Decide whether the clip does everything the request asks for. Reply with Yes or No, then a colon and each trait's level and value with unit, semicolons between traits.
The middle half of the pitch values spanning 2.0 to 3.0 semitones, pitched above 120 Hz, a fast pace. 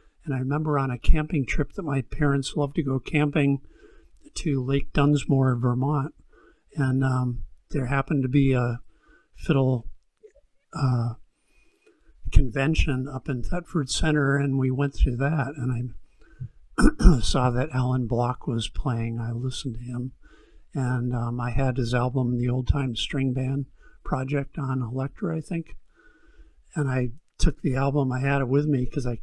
No: narrow, 2.5 semitones; low, 135 Hz; average, 160 wpm